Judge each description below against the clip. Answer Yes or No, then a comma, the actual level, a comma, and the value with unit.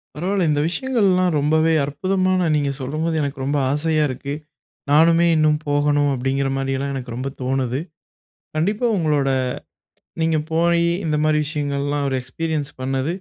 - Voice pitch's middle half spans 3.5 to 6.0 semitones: No, average, 3.1 semitones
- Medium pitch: Yes, medium, 150 Hz